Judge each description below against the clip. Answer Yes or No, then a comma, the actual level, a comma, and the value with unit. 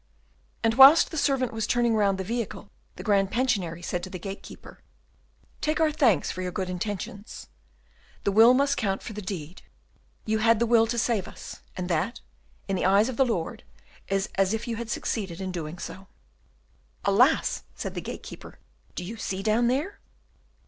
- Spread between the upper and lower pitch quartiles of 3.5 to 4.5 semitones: Yes, average, 4.0 semitones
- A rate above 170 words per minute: Yes, average, 185 wpm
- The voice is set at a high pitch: Yes, high, 215 Hz